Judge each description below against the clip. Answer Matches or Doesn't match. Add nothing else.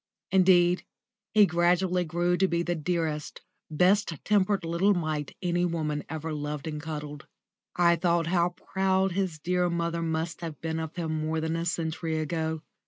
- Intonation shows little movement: Matches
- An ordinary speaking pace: Matches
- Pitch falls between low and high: Matches